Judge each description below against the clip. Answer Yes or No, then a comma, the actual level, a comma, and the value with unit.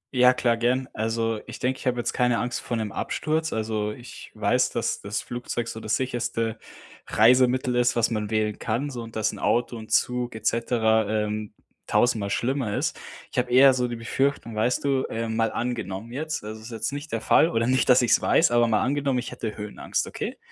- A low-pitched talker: Yes, low, 120 Hz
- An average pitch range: No, narrow, 2.2 semitones